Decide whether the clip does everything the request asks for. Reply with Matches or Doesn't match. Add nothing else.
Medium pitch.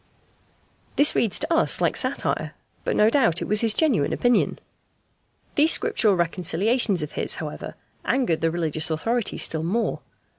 Doesn't match